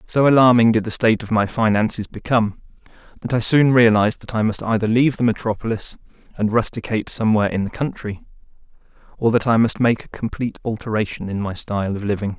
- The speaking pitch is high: No, low, 110 Hz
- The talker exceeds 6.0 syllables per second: Yes, 6.5 syllables/s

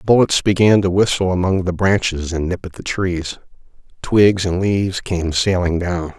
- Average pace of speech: Yes, average, 175 wpm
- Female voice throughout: No, male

